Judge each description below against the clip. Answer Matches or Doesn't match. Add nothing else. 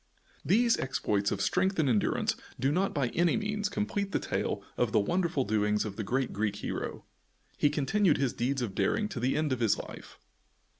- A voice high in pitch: Doesn't match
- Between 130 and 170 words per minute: Doesn't match